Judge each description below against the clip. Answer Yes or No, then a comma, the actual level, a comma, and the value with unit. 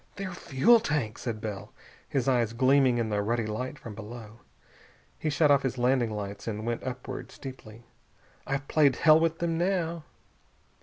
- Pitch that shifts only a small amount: No, average, 4.8 semitones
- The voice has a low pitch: Yes, low, 130 Hz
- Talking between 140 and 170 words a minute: Yes, average, 165 wpm